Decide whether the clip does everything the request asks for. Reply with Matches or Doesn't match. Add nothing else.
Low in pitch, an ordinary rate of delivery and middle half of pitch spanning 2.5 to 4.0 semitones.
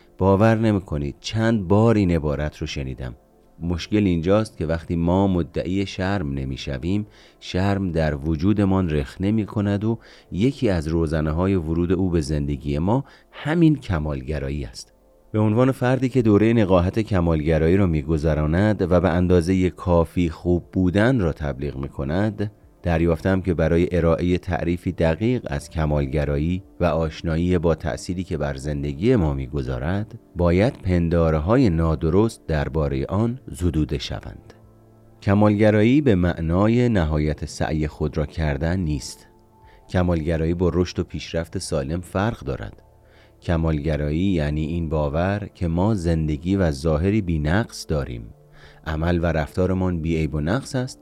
Doesn't match